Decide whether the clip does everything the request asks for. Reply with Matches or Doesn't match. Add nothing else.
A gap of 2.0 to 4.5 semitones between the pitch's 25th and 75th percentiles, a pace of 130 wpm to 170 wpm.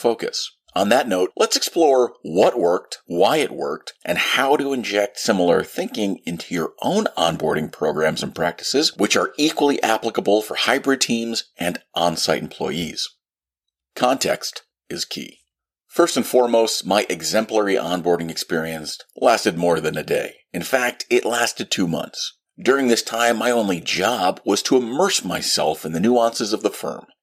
Doesn't match